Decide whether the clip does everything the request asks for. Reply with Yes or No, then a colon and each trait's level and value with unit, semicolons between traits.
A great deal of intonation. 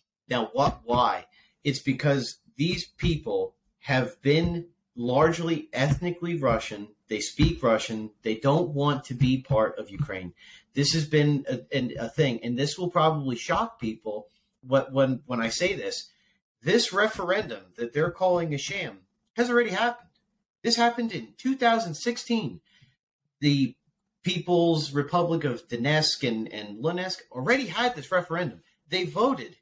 Yes: wide, 5.7 semitones